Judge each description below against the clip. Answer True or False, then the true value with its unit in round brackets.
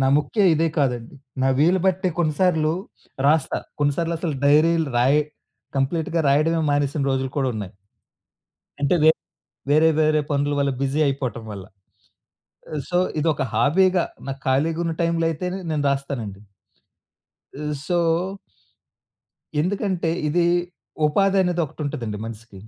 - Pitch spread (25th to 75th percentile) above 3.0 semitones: True (3.5 semitones)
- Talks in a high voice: False (150 Hz)